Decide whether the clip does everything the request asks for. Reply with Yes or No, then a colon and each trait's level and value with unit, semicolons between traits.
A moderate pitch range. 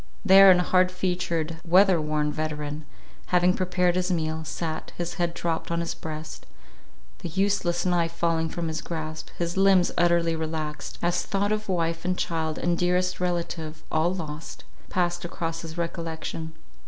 No: narrow, 2.0 semitones